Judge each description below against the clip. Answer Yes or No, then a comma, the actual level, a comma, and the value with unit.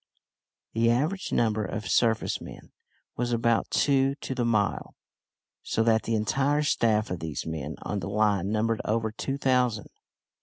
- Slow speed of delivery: No, average, 155 wpm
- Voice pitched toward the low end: Yes, low, 115 Hz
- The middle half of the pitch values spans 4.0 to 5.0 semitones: No, average, 2.8 semitones